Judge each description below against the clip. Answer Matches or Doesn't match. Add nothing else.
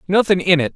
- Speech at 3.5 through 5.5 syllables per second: Doesn't match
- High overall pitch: Doesn't match